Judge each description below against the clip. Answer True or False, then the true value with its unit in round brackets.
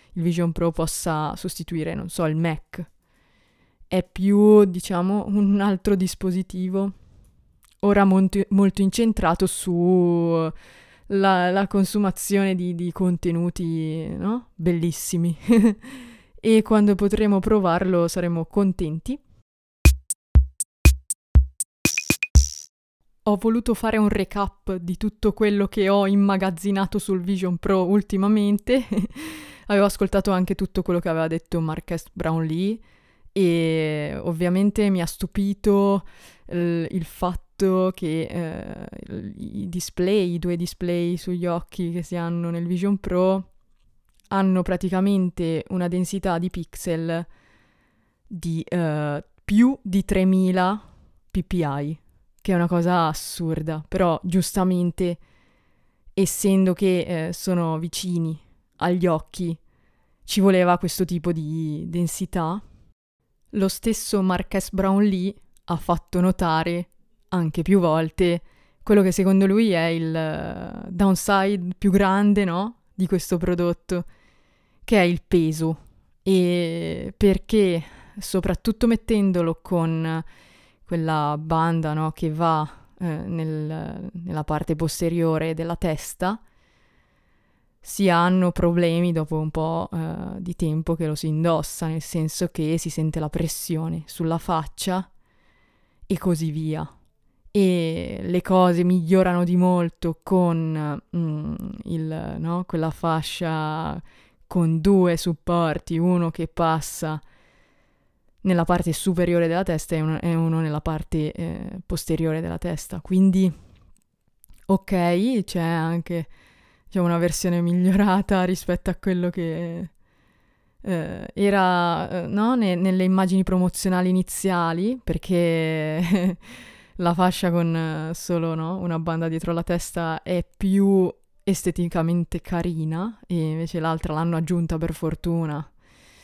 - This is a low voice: False (175 Hz)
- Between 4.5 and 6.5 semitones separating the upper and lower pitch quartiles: False (2.7 semitones)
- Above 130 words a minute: False (115 wpm)